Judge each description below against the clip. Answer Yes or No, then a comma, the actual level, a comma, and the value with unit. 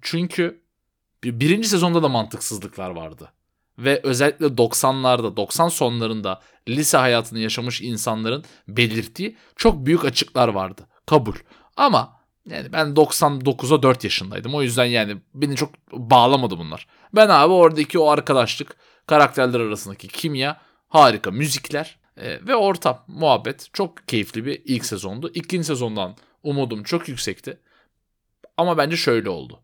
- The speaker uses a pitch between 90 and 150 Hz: Yes, low, 135 Hz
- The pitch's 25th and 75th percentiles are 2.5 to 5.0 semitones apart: No, wide, 5.4 semitones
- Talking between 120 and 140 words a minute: Yes, average, 125 wpm